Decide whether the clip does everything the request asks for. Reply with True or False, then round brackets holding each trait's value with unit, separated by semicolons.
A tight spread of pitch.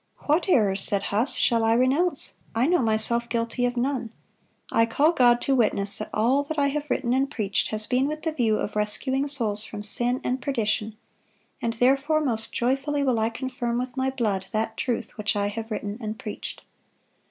False (3.8 semitones)